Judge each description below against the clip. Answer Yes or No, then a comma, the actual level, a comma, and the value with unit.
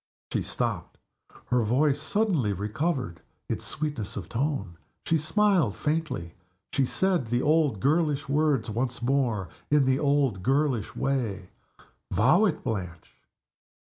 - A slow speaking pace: Yes, slow, 125 wpm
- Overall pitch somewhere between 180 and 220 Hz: No, low, 135 Hz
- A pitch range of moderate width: No, wide, 5.8 semitones